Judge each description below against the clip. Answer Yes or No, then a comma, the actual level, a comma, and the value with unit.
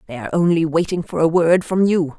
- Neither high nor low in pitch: Yes, medium, 165 Hz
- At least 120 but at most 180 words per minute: No, fast, 245 wpm